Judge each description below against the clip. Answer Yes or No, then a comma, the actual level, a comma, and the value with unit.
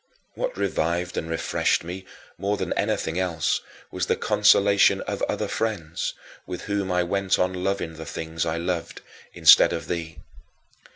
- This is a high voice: No, very low, 90 Hz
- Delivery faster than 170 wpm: No, average, 155 wpm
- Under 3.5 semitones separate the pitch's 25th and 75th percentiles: Yes, average, 3.0 semitones